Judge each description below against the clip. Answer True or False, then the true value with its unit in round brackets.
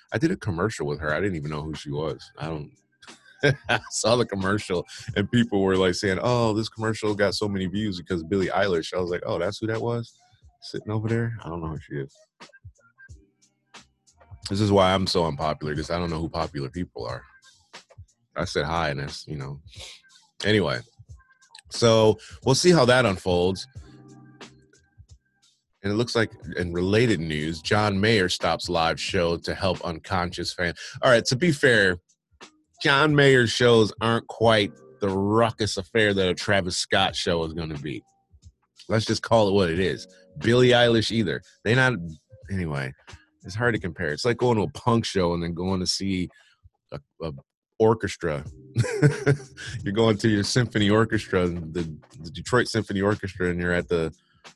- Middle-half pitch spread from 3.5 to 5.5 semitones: True (4.7 semitones)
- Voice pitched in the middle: False (100 Hz)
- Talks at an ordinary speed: True (180 wpm)